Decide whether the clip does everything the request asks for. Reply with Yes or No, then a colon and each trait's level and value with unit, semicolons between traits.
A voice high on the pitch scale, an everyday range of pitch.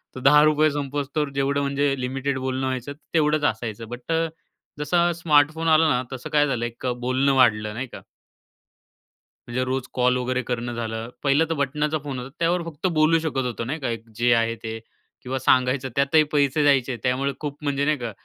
No: low, 135 Hz; average, 3.0 semitones